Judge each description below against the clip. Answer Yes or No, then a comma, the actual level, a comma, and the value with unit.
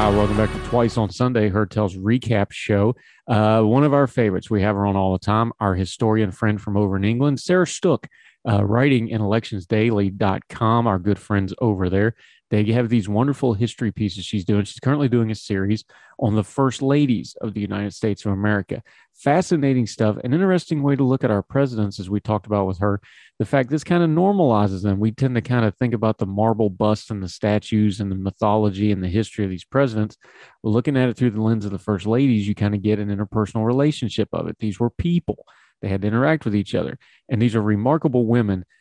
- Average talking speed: No, fast, 220 wpm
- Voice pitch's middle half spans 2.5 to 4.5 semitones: Yes, average, 3.0 semitones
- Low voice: Yes, low, 110 Hz